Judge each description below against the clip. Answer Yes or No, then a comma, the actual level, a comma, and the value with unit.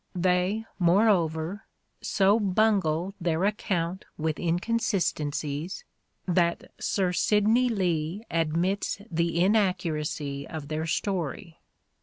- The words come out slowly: Yes, slow, 90 wpm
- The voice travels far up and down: No, average, 3.7 semitones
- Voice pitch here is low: No, medium, 180 Hz